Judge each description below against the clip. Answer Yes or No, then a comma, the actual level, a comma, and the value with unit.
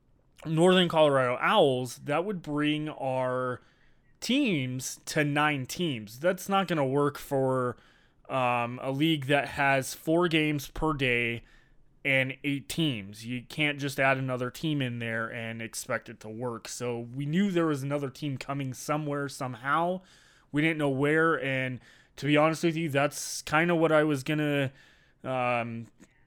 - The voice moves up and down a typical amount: Yes, average, 3.3 semitones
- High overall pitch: No, medium, 140 Hz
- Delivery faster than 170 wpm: No, average, 160 wpm